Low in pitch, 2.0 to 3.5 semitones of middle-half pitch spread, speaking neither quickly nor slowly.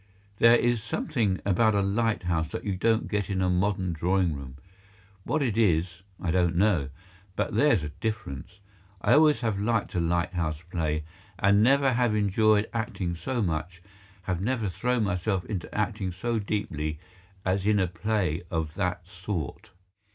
No: low, 100 Hz; average, 4.2 semitones; average, 160 wpm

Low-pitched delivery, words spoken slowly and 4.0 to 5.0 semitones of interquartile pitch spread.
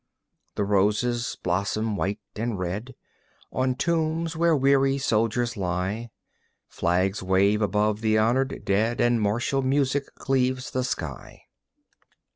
Yes: low, 115 Hz; slow, 115 wpm; average, 4.5 semitones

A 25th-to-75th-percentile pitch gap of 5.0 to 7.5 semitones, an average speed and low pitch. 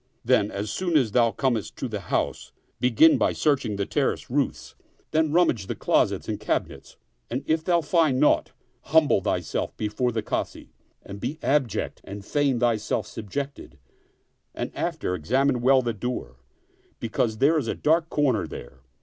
Yes: wide, 5.5 semitones; average, 160 wpm; low, 125 Hz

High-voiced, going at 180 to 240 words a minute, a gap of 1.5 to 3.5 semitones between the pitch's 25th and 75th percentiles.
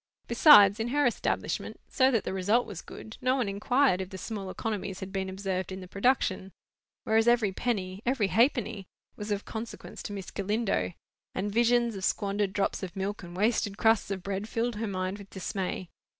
Yes: high, 205 Hz; average, 185 wpm; average, 3.2 semitones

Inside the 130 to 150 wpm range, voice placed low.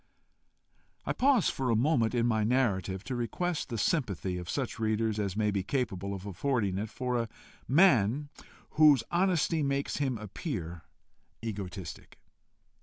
Yes: average, 145 wpm; low, 115 Hz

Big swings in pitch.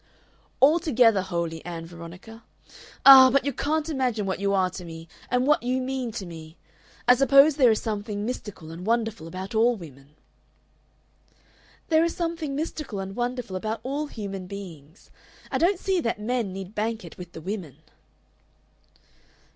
Yes: wide, 6.1 semitones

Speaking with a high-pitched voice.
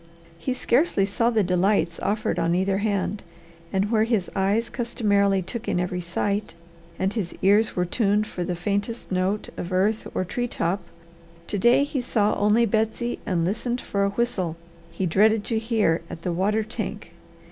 Yes: high, 205 Hz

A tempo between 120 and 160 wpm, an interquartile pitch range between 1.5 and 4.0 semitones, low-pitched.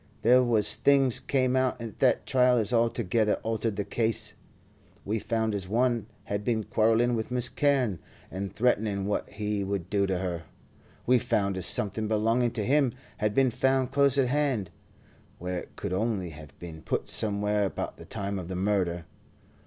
No: average, 175 wpm; average, 3.7 semitones; low, 110 Hz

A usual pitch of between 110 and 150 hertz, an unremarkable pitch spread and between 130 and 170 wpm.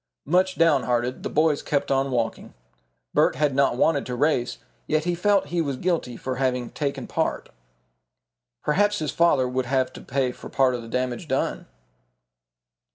Yes: low, 135 Hz; average, 4.1 semitones; average, 165 wpm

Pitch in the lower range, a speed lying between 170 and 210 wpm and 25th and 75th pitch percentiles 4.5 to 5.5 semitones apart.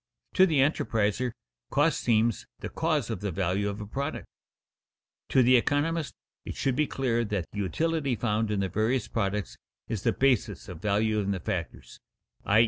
Yes: low, 115 Hz; average, 175 wpm; average, 4.9 semitones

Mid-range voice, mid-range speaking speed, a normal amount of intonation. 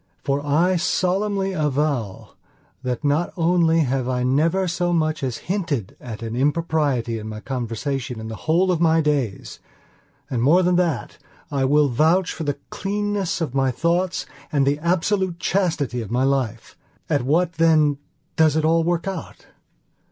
Yes: medium, 155 Hz; average, 160 wpm; average, 4.7 semitones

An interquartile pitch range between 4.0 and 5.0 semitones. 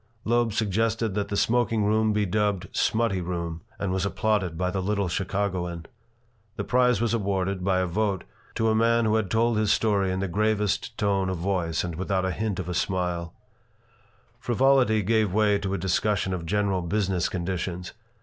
No: average, 2.9 semitones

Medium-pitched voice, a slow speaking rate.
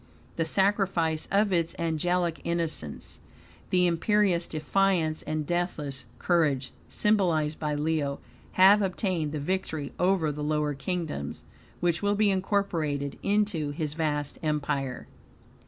Yes: medium, 165 Hz; slow, 120 wpm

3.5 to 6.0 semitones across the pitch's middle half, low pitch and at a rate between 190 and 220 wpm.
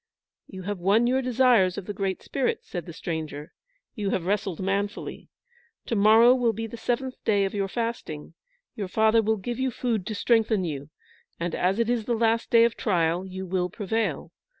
No: average, 3.8 semitones; high, 205 Hz; average, 195 wpm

